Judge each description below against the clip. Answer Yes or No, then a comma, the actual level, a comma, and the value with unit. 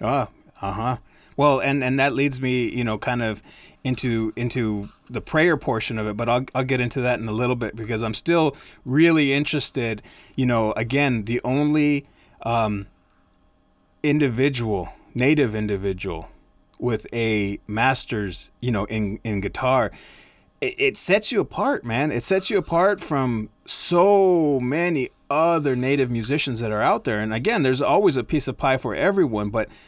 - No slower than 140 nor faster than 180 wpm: Yes, average, 165 wpm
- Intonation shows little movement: No, average, 4.6 semitones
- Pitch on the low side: Yes, low, 125 Hz